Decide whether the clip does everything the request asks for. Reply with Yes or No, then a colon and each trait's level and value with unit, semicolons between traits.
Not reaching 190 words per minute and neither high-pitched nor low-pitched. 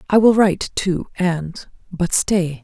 Yes: slow, 135 wpm; medium, 180 Hz